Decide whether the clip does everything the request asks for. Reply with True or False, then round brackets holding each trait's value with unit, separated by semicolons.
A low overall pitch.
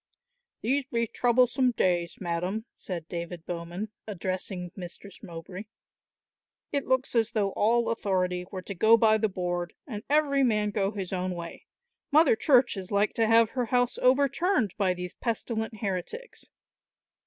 False (210 Hz)